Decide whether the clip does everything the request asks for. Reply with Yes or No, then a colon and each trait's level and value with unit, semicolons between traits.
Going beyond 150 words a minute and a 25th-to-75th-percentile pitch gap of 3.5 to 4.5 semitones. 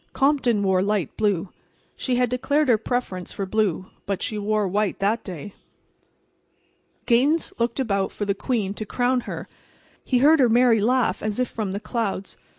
Yes: average, 170 wpm; average, 3.9 semitones